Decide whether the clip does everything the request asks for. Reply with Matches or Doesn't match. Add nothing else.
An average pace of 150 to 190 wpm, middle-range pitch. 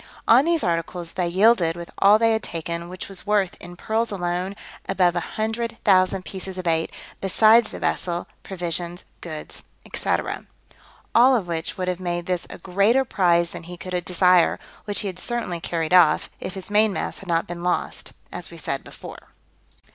Matches